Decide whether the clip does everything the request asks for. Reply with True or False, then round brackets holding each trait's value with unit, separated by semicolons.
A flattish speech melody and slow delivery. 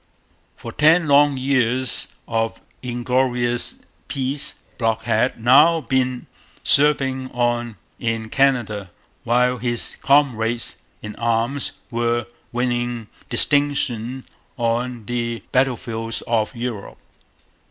True (2.2 semitones; 95 wpm)